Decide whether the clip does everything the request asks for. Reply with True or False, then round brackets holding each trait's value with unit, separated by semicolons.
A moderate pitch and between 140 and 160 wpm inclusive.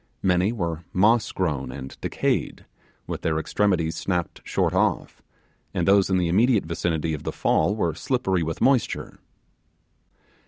False (90 Hz; 145 wpm)